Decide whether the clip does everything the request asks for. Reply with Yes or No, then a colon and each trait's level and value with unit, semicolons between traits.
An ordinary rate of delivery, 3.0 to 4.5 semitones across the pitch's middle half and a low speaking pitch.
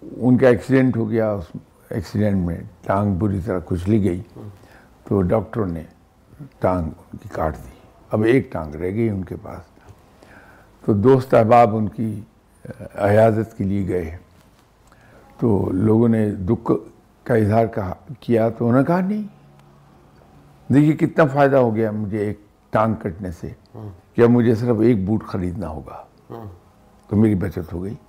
Yes: average, 155 wpm; average, 3.7 semitones; low, 105 Hz